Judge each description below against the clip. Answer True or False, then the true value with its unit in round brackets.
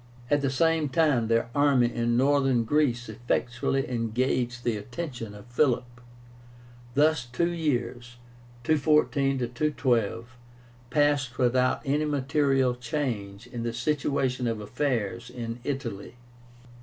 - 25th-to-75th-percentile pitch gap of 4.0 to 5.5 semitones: False (3.3 semitones)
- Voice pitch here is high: False (125 Hz)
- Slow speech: True (115 wpm)